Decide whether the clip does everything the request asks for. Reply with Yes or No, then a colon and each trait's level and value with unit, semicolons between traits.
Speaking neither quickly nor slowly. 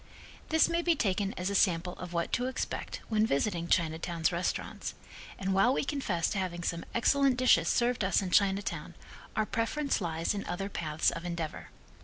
Yes: average, 180 wpm